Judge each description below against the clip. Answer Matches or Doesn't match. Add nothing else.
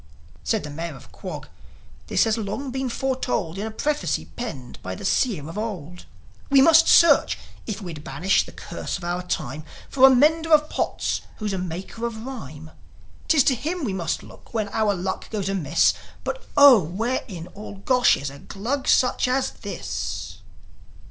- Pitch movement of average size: Doesn't match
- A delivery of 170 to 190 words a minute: Matches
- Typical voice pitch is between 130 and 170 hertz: Doesn't match